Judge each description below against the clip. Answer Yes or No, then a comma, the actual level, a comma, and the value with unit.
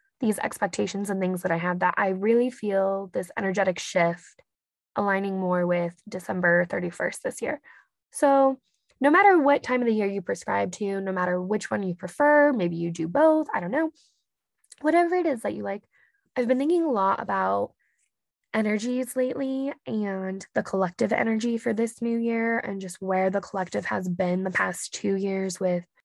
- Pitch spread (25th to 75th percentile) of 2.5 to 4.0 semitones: No, average, 5.2 semitones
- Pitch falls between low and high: No, high, 200 Hz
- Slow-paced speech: No, average, 180 wpm